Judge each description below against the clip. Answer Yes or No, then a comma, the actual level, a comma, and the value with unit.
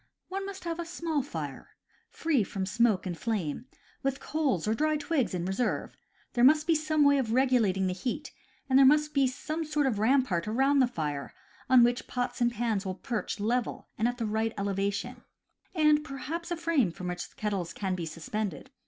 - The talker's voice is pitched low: No, high, 245 Hz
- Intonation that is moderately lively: No, wide, 6.7 semitones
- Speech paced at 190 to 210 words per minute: Yes, average, 195 wpm